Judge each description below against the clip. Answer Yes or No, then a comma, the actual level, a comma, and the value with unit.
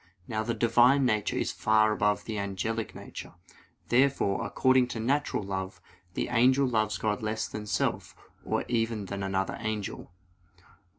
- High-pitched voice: No, low, 110 Hz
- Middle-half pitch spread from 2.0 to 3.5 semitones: Yes, narrow, 2.6 semitones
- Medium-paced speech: Yes, average, 150 wpm